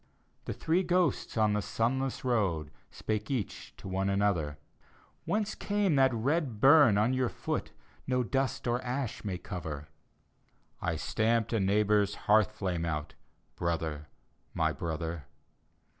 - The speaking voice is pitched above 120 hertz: No, low, 105 Hz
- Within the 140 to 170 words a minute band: Yes, average, 145 wpm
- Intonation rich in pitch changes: Yes, wide, 6.3 semitones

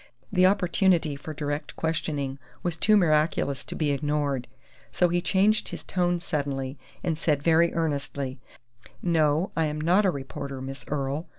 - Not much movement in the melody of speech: No, average, 3.6 semitones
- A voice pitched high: No, medium, 155 Hz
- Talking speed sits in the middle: Yes, average, 155 wpm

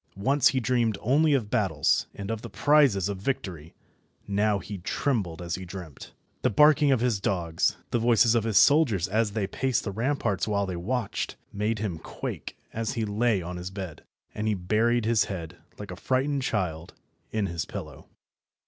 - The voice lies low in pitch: Yes, low, 105 Hz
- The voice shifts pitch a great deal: No, average, 4.3 semitones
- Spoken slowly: No, average, 185 wpm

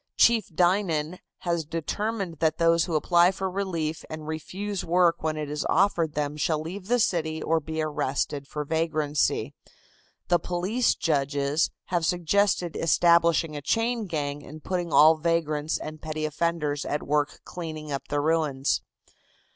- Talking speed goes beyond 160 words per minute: No, average, 150 wpm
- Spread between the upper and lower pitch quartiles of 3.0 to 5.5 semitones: No, narrow, 2.6 semitones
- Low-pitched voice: No, medium, 160 Hz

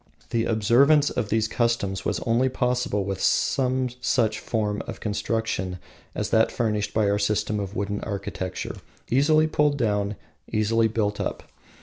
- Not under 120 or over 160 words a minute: Yes, average, 140 wpm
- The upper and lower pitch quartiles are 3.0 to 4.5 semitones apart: Yes, average, 3.3 semitones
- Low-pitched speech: Yes, low, 110 Hz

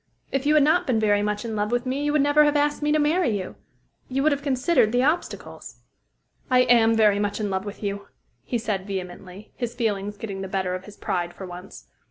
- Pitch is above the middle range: Yes, high, 225 Hz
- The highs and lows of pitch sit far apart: Yes, wide, 5.7 semitones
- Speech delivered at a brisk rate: Yes, fast, 235 wpm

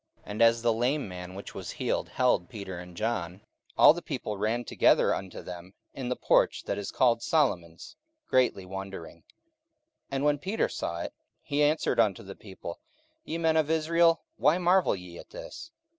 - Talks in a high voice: No, low, 115 Hz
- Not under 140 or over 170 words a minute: No, average, 185 wpm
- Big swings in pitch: Yes, wide, 8.2 semitones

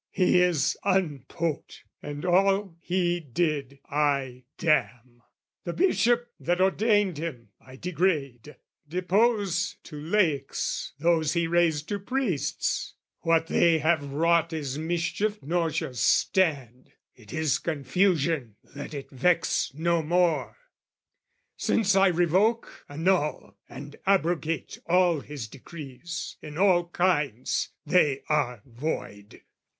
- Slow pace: Yes, slow, 115 wpm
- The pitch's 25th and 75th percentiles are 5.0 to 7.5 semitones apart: No, average, 4.0 semitones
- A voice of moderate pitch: Yes, medium, 165 Hz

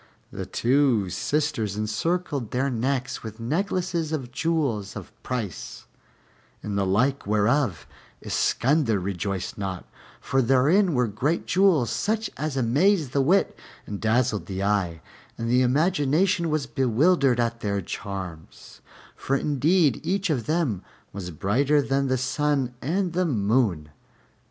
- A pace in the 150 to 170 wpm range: No, slow, 135 wpm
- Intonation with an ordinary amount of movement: No, wide, 6.3 semitones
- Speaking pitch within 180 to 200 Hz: No, low, 130 Hz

